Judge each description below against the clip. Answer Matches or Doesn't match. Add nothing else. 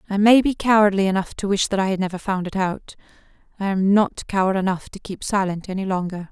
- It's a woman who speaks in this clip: Matches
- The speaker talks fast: Matches